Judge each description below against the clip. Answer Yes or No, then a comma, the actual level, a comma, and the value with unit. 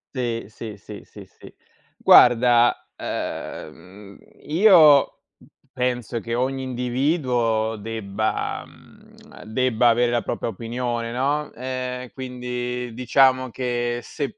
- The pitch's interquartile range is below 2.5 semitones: Yes, narrow, 1.9 semitones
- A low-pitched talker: Yes, low, 125 Hz